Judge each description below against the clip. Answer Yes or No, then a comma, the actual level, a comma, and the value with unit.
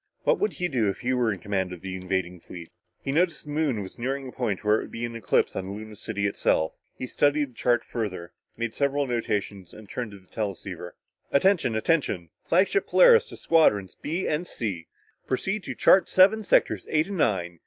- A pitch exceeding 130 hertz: No, low, 115 Hz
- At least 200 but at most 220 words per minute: Yes, fast, 205 wpm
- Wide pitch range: Yes, wide, 7.6 semitones